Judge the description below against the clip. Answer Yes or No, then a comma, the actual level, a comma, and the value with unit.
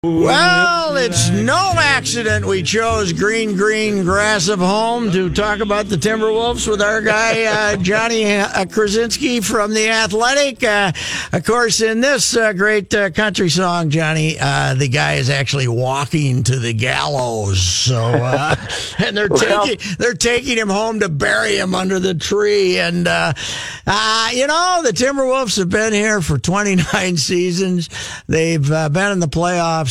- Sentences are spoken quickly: No, average, 160 wpm